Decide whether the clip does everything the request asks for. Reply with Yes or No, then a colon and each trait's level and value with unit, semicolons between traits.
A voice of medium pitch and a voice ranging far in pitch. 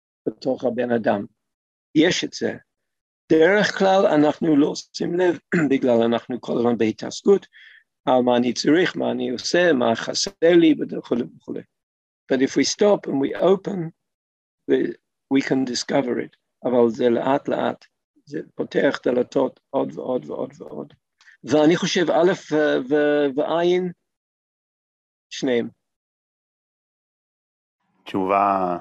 Yes: medium, 145 Hz; wide, 6.2 semitones